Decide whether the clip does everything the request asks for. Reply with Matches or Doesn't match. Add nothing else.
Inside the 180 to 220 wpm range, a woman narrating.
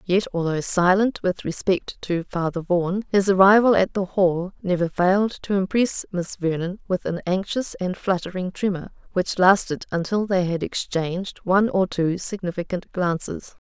Doesn't match